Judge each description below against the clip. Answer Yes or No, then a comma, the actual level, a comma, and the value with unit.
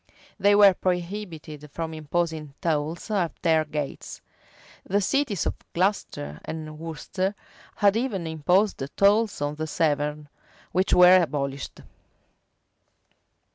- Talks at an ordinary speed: No, slow, 115 wpm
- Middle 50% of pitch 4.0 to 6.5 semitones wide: Yes, average, 4.5 semitones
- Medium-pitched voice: Yes, medium, 170 Hz